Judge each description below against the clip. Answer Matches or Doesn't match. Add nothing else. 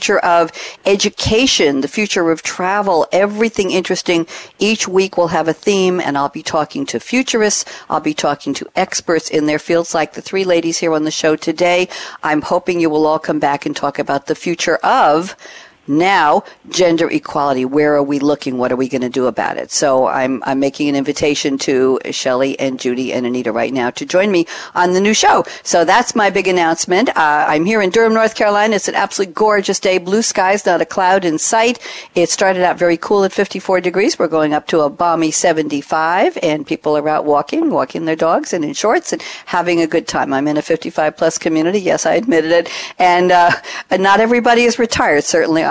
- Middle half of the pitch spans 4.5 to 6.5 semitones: Doesn't match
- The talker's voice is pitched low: Doesn't match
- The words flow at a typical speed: Doesn't match